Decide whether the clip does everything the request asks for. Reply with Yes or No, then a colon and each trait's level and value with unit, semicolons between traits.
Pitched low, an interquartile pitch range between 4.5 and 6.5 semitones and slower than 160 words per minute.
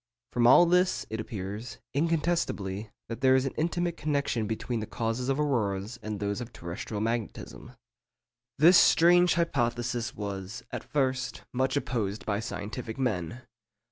Yes: low, 120 Hz; average, 4.9 semitones; average, 140 wpm